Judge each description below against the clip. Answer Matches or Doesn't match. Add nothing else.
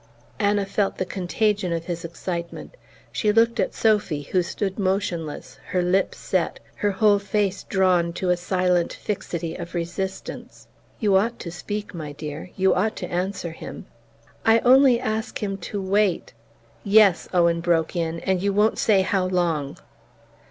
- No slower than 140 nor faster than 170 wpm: Matches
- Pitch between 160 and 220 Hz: Matches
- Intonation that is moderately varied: Matches